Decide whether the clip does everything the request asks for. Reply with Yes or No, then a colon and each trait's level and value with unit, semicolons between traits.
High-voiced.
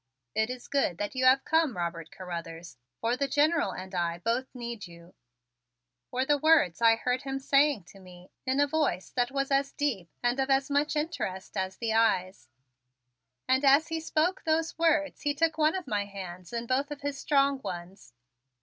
Yes: very high, 255 Hz